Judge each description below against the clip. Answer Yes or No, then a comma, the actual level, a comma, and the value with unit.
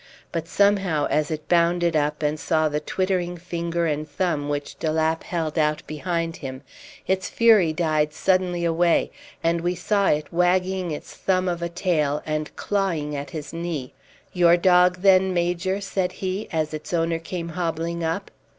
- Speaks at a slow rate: No, average, 170 wpm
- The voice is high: No, medium, 170 Hz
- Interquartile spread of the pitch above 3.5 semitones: No, average, 2.8 semitones